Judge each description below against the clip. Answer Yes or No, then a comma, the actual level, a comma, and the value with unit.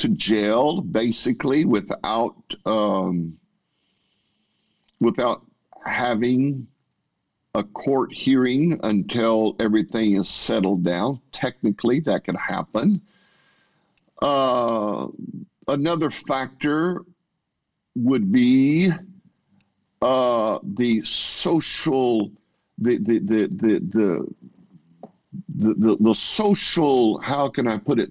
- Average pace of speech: No, slow, 85 wpm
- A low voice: Yes, low, 130 Hz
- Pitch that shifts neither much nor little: No, wide, 7.6 semitones